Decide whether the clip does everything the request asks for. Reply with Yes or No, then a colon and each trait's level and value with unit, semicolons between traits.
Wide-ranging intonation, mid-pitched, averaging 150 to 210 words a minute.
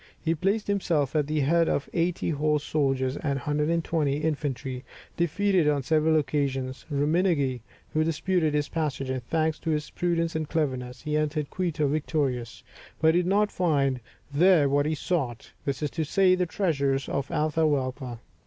No: average, 3.0 semitones; medium, 150 Hz; average, 165 wpm